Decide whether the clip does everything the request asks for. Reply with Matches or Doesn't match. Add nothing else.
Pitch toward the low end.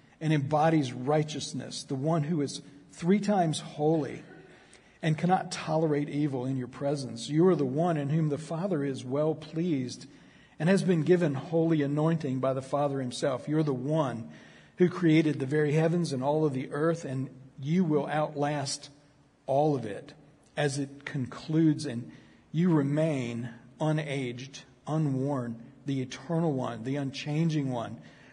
Doesn't match